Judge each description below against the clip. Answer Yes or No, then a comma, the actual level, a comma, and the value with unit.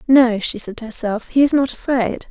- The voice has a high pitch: Yes, high, 240 Hz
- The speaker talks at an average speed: No, fast, 235 wpm